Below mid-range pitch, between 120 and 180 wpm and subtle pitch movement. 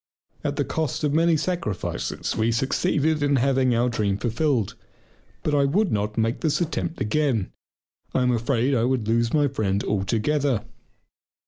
No: low, 130 Hz; average, 155 wpm; average, 5.0 semitones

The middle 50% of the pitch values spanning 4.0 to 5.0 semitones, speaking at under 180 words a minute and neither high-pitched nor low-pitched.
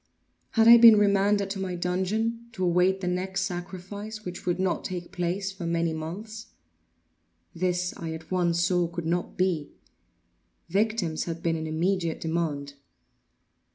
No: average, 2.7 semitones; average, 150 wpm; medium, 180 Hz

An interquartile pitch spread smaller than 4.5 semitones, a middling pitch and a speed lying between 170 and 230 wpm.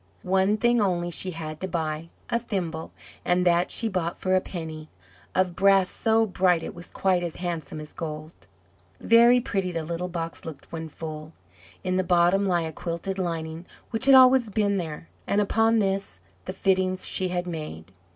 Yes: average, 3.0 semitones; medium, 180 Hz; average, 180 wpm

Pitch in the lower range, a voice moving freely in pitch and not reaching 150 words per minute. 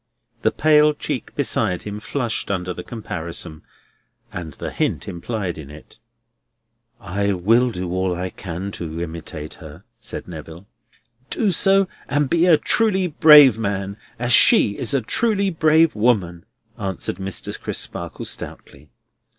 Yes: low, 100 Hz; wide, 8.7 semitones; average, 140 wpm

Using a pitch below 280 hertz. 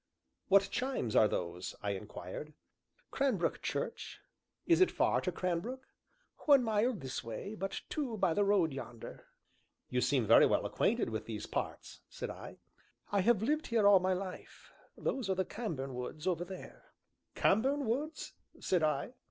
Yes: high, 190 Hz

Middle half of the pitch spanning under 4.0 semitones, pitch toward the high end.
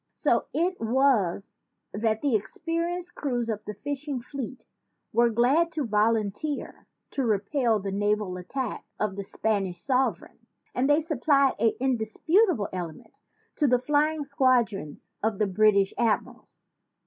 No: average, 5.3 semitones; high, 240 Hz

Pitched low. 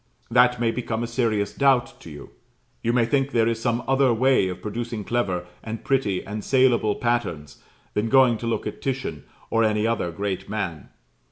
Yes: low, 115 Hz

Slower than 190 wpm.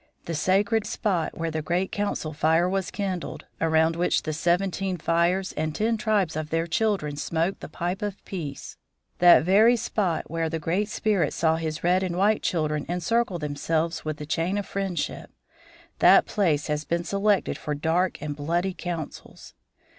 Yes: average, 170 wpm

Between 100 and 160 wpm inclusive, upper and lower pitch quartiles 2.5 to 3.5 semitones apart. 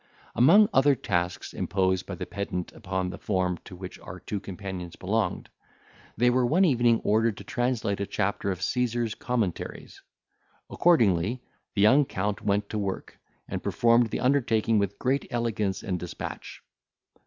No: average, 155 wpm; average, 4.3 semitones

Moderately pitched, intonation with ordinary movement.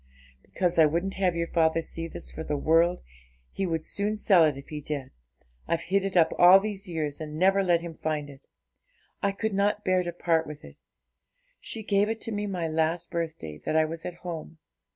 Yes: medium, 170 Hz; average, 3.5 semitones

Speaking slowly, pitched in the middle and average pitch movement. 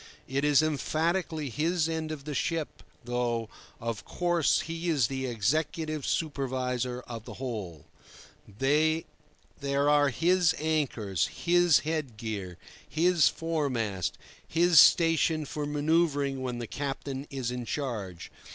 Yes: slow, 120 wpm; medium, 145 Hz; average, 4.5 semitones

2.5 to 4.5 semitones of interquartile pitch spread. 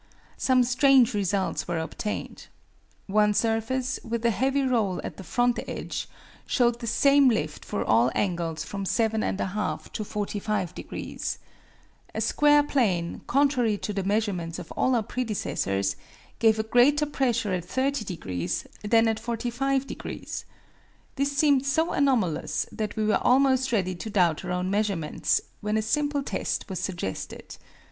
No: wide, 5.5 semitones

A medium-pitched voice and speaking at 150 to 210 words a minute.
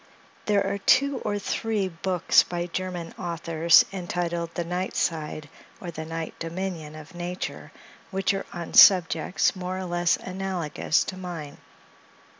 No: medium, 175 Hz; average, 140 wpm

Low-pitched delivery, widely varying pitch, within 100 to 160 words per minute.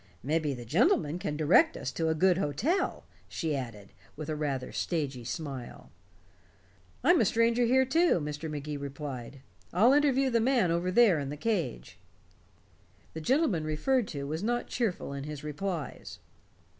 No: medium, 160 Hz; wide, 8.2 semitones; average, 155 wpm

